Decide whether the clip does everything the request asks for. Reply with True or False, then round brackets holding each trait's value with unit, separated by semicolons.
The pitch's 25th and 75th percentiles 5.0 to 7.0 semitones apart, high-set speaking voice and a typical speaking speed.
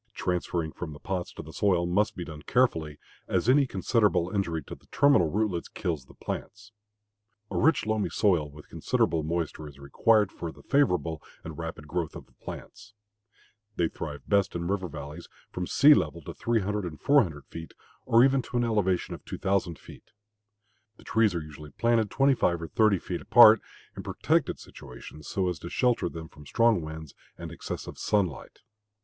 False (5.3 semitones; 90 Hz; 180 wpm)